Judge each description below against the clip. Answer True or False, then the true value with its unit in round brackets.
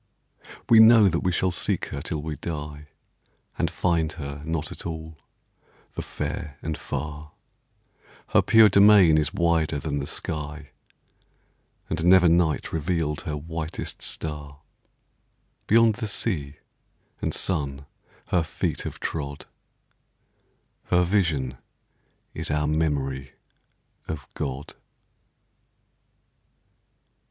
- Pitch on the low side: True (80 Hz)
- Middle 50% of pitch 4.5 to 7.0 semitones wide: False (3.0 semitones)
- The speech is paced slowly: True (110 wpm)